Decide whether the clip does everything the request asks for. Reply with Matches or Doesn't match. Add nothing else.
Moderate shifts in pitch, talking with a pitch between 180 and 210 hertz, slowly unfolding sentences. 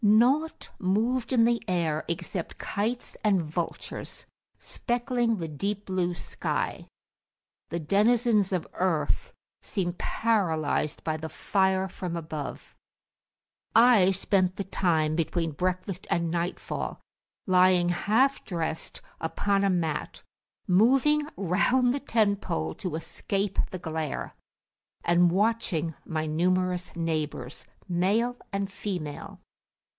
Matches